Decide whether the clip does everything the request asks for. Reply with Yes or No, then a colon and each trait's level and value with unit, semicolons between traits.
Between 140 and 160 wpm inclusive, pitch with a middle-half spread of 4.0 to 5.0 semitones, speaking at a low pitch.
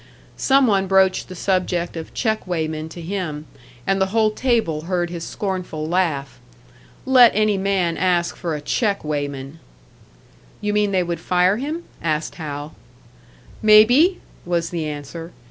No: average, 145 wpm; average, 4.4 semitones; medium, 180 Hz